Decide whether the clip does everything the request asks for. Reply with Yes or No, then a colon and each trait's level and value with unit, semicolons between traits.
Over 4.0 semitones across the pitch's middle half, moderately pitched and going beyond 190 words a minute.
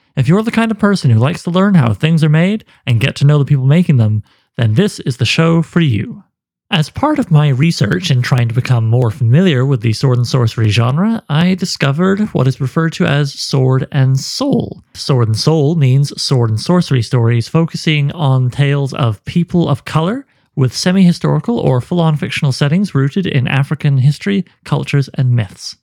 Yes: average, 4.7 semitones; medium, 145 Hz; average, 200 wpm